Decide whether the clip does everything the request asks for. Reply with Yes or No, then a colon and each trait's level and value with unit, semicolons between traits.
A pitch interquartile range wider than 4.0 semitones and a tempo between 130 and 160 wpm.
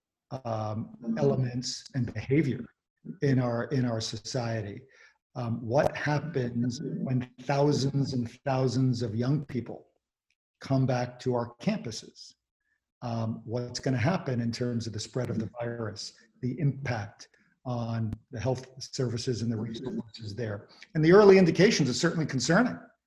No: average, 3.0 semitones; average, 140 wpm